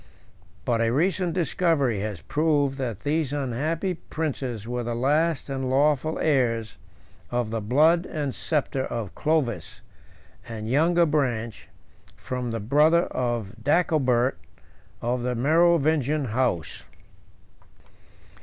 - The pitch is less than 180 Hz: Yes, low, 135 Hz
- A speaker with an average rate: No, slow, 115 wpm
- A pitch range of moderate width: Yes, average, 4.8 semitones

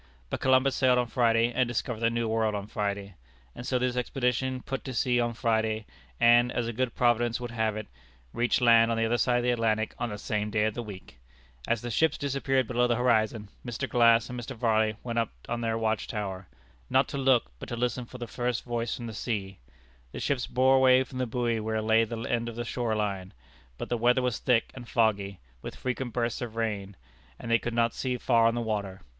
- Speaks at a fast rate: Yes, fast, 230 wpm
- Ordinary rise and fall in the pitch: No, narrow, 1.9 semitones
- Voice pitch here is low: Yes, low, 115 Hz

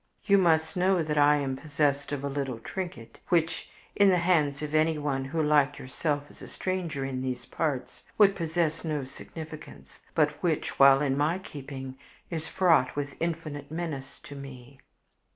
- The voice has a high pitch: No, medium, 150 Hz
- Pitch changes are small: No, average, 3.1 semitones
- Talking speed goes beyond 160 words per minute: Yes, average, 170 wpm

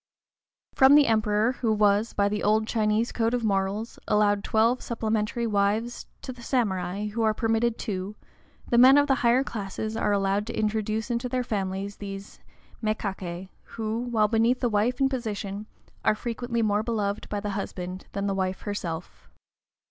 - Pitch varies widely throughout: No, narrow, 2.5 semitones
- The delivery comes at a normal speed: Yes, average, 170 wpm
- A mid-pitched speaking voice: No, high, 215 Hz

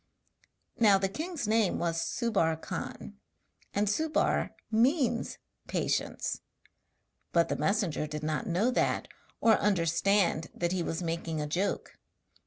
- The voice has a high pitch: Yes, high, 195 Hz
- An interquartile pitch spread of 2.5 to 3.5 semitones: No, average, 5.2 semitones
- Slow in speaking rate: Yes, slow, 125 wpm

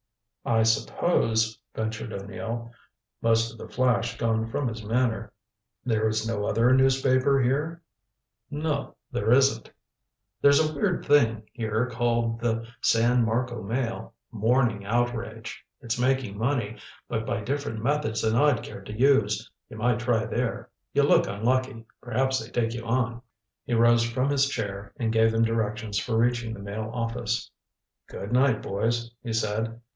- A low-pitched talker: Yes, low, 115 Hz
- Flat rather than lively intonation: Yes, narrow, 2.1 semitones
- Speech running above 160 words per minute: No, average, 155 wpm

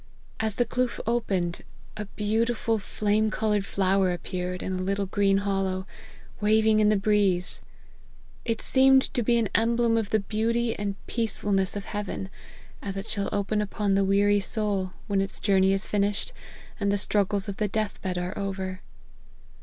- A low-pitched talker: No, high, 205 Hz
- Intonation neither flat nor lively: No, narrow, 2.0 semitones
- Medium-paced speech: Yes, average, 170 wpm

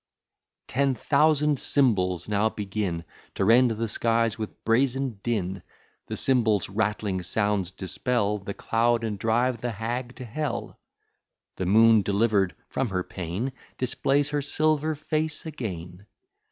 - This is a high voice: No, low, 115 Hz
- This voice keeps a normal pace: No, slow, 130 wpm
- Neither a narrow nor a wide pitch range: Yes, average, 4.5 semitones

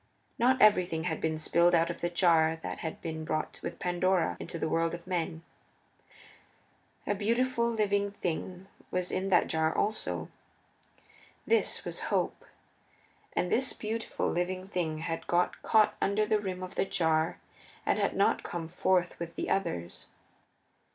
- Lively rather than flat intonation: No, average, 3.5 semitones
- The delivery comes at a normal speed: Yes, average, 155 wpm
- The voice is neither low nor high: Yes, medium, 180 Hz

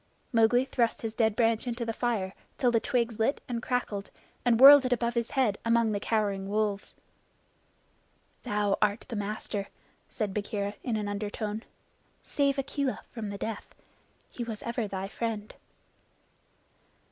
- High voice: Yes, high, 225 Hz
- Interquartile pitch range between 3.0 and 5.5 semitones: No, narrow, 2.6 semitones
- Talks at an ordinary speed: Yes, average, 150 wpm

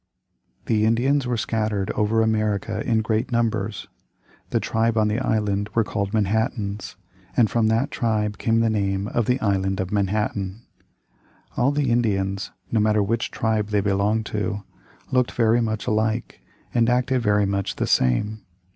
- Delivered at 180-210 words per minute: No, average, 155 wpm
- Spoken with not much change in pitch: Yes, narrow, 2.0 semitones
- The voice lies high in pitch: No, low, 110 Hz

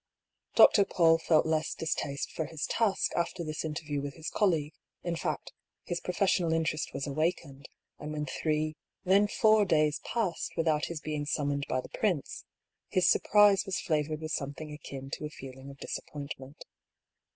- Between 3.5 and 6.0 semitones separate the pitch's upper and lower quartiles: No, average, 2.8 semitones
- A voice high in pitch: No, medium, 155 Hz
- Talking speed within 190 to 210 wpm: No, average, 160 wpm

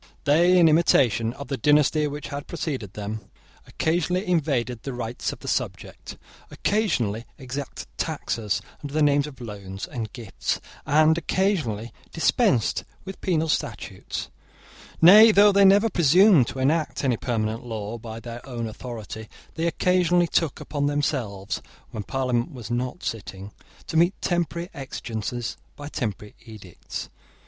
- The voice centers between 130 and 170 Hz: Yes, low, 135 Hz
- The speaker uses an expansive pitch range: Yes, wide, 6.4 semitones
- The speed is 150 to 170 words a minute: No, average, 140 wpm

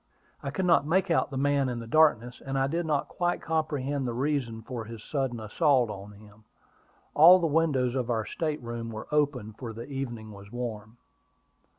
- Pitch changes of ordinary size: Yes, average, 4.5 semitones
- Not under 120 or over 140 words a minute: No, average, 195 wpm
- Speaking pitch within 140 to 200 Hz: No, low, 130 Hz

